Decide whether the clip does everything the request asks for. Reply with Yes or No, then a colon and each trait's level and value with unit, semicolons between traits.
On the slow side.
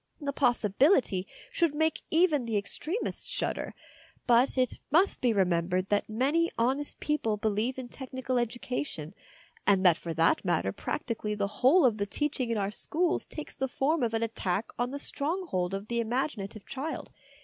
No: average, 170 wpm